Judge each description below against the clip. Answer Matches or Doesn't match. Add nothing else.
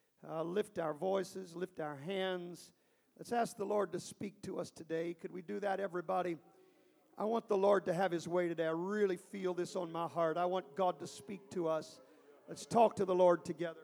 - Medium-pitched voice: Matches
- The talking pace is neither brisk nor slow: Doesn't match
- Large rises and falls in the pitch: Doesn't match